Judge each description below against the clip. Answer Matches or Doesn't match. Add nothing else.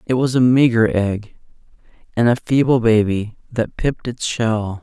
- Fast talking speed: Doesn't match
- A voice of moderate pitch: Doesn't match